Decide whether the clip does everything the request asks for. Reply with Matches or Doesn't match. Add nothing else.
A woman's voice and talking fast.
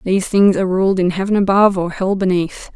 Matches